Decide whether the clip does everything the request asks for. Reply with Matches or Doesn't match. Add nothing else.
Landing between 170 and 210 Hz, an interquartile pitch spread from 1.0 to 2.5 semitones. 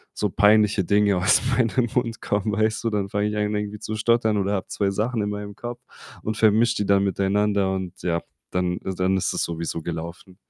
Doesn't match